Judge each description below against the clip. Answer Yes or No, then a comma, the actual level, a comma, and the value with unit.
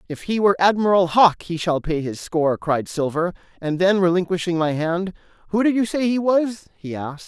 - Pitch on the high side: No, medium, 180 Hz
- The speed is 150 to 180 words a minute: No, fast, 205 wpm